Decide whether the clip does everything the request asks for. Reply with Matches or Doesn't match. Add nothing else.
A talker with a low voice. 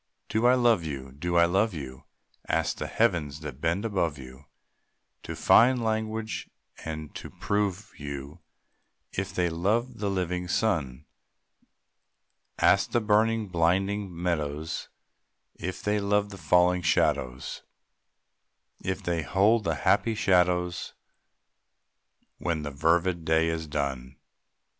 Matches